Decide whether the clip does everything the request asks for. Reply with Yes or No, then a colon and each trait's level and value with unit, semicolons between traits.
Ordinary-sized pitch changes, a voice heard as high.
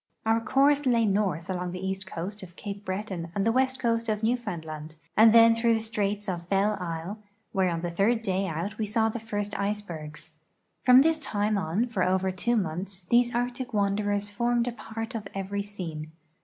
Yes: average, 3.6 semitones; high, 205 Hz